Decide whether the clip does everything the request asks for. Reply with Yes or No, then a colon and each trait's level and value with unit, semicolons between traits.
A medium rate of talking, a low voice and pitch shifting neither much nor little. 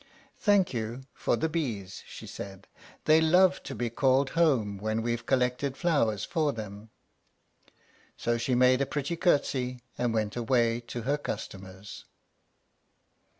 Yes: average, 145 wpm; low, 125 Hz; average, 4.7 semitones